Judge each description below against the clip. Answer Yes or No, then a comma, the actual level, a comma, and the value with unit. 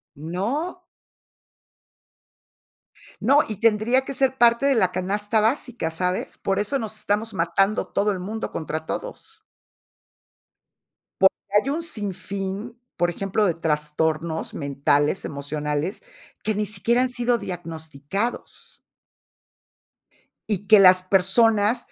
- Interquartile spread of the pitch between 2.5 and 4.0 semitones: No, average, 5.2 semitones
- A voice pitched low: No, high, 200 Hz